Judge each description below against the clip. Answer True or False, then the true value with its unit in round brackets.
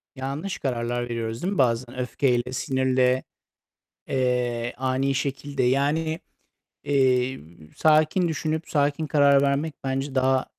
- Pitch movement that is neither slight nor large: False (2.2 semitones)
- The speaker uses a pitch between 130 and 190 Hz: True (135 Hz)